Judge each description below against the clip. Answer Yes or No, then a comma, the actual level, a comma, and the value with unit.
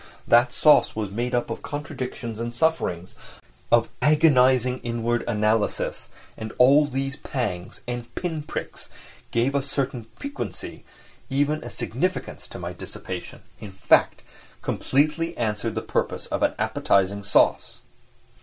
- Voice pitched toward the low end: Yes, low, 125 Hz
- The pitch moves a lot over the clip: No, average, 4.3 semitones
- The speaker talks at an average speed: No, slow, 125 wpm